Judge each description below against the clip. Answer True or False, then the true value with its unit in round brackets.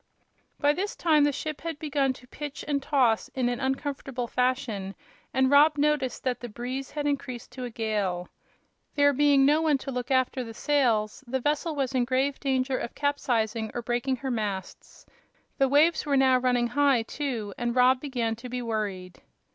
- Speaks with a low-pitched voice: False (260 Hz)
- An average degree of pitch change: True (3.0 semitones)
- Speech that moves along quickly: False (185 wpm)